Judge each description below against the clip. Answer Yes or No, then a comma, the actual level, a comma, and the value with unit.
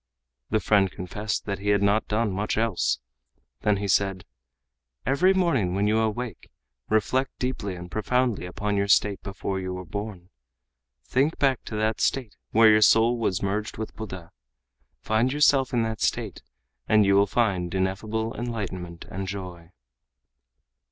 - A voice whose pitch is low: Yes, low, 105 Hz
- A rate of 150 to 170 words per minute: Yes, average, 155 wpm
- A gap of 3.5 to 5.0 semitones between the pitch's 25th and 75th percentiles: No, average, 2.7 semitones